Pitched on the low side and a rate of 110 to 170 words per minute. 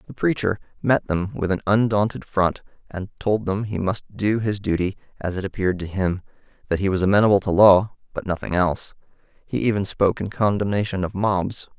No: low, 100 Hz; average, 190 wpm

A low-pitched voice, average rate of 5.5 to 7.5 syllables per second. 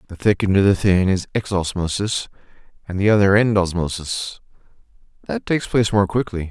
Yes: low, 100 Hz; 5.6 syllables/s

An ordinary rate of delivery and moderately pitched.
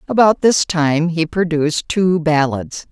Yes: average, 145 wpm; medium, 170 Hz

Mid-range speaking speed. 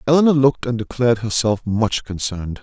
Yes: average, 160 wpm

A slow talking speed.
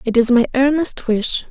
No: average, 200 wpm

